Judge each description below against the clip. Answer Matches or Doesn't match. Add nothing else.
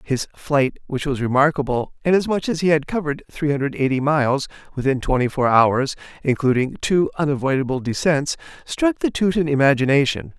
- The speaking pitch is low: Doesn't match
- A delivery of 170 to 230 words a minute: Doesn't match